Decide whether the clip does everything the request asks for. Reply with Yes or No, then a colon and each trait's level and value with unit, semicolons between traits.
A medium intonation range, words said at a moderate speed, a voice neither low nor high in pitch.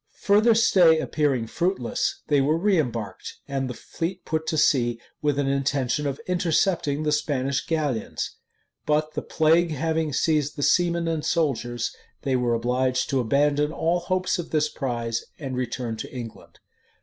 Yes: average, 4.1 semitones; average, 155 wpm; medium, 150 Hz